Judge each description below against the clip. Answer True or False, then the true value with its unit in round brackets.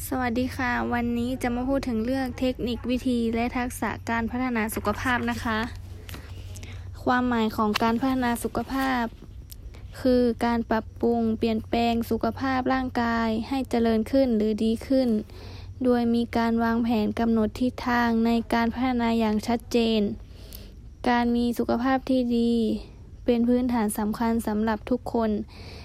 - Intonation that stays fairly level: True (1.9 semitones)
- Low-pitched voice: False (235 Hz)